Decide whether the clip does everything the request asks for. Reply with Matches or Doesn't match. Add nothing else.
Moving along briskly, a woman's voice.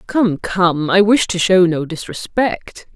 Doesn't match